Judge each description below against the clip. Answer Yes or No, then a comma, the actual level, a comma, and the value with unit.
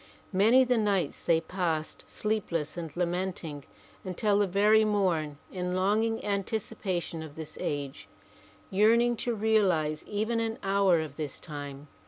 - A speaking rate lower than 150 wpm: Yes, average, 140 wpm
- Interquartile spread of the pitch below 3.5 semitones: No, average, 5.0 semitones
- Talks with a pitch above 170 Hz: Yes, high, 190 Hz